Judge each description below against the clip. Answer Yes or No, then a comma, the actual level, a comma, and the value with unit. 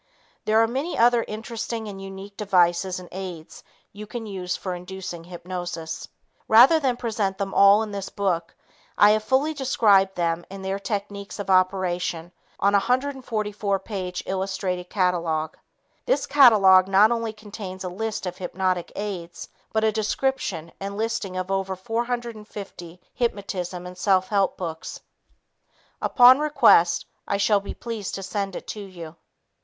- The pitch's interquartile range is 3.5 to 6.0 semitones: No, average, 3.1 semitones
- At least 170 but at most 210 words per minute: No, average, 150 wpm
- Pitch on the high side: Yes, high, 195 Hz